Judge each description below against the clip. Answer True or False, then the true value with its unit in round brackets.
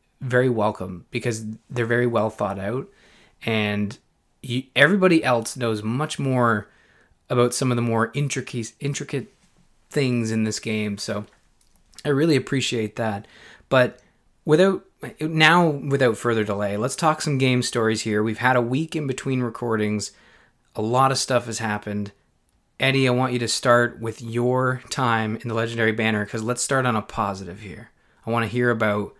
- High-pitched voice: False (120 Hz)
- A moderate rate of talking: True (165 wpm)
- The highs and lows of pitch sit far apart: False (3.1 semitones)